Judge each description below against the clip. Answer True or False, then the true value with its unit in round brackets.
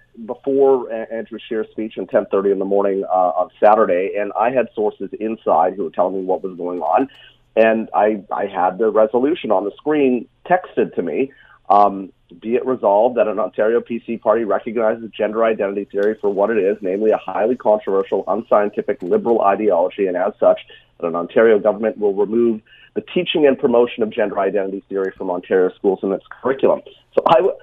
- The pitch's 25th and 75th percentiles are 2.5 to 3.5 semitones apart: False (3.9 semitones)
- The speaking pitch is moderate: False (110 Hz)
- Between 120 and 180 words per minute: False (190 wpm)